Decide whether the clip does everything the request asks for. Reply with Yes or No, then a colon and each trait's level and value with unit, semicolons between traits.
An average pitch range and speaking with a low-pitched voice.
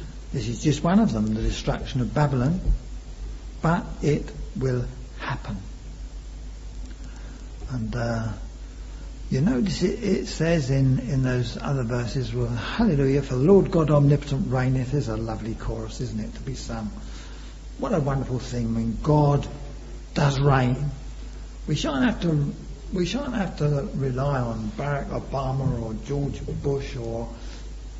Yes: average, 3.9 semitones; low, 130 Hz